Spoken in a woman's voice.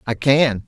No: male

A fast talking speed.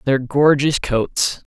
No: slow, 120 wpm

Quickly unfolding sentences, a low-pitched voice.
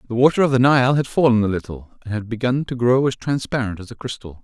Yes: fast, 255 wpm; low, 120 Hz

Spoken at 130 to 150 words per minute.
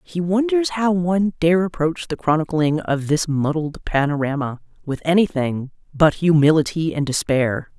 Yes: average, 140 wpm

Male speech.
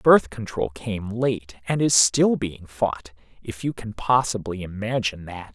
Yes: male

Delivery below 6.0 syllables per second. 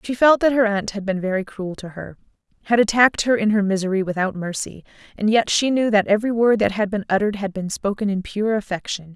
No: 6.1 syllables/s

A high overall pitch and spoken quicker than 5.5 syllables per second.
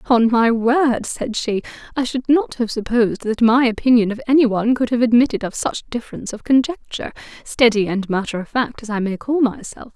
Yes: high, 235 Hz; 5.7 syllables/s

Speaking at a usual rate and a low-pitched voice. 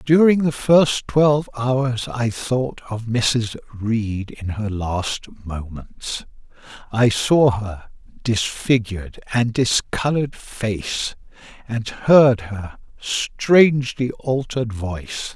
No: slow, 105 wpm; low, 120 Hz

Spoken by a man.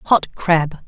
No: female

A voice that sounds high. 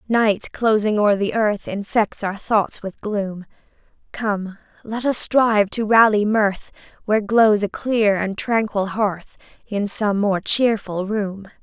Yes: high, 210 Hz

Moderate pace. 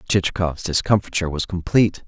No: slow, 115 wpm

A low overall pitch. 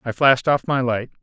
Yes: low, 130 Hz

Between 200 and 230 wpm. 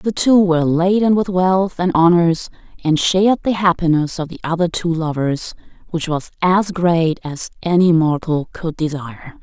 No: average, 165 wpm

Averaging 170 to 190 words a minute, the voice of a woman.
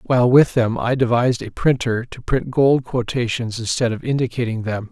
No: average, 185 wpm; male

